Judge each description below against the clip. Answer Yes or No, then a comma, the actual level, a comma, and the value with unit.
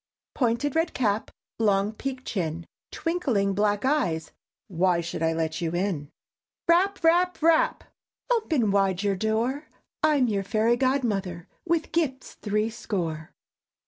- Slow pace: Yes, slow, 130 wpm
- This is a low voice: No, high, 220 Hz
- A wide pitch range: Yes, wide, 7.3 semitones